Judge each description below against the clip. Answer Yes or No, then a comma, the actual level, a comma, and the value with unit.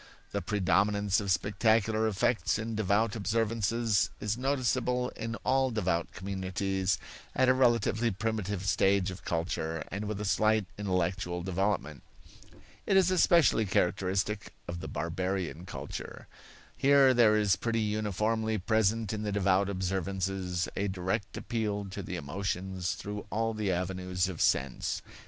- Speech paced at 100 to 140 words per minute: Yes, slow, 135 wpm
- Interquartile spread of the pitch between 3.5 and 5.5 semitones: No, average, 3.0 semitones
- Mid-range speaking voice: No, low, 100 Hz